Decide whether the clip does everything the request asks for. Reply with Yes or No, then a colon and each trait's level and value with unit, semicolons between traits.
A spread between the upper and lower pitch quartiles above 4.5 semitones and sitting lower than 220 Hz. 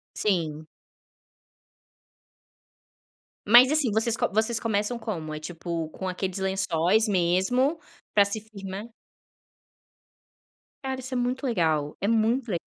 Yes: average, 5.0 semitones; high, 205 Hz